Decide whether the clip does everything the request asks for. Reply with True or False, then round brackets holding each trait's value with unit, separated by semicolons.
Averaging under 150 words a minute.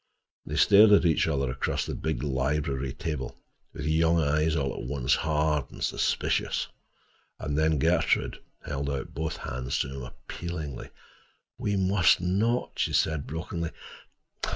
True (140 wpm)